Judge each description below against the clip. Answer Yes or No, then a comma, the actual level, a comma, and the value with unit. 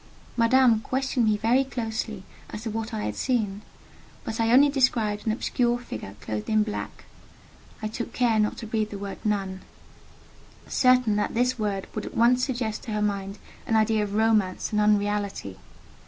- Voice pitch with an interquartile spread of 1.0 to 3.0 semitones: Yes, narrow, 2.4 semitones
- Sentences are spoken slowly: No, average, 175 wpm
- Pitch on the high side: Yes, high, 220 Hz